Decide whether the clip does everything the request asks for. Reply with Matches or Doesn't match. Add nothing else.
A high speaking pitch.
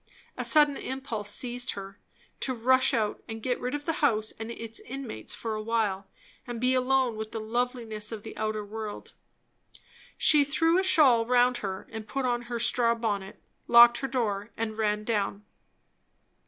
Matches